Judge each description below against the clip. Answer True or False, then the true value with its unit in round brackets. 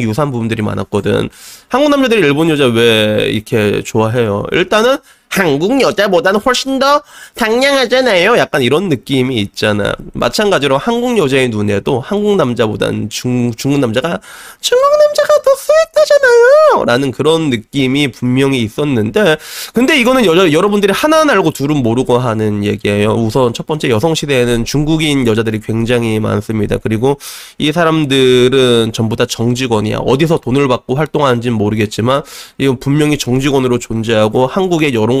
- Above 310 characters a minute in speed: True (365 characters per minute)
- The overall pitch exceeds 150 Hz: False (135 Hz)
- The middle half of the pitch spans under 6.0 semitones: False (7.2 semitones)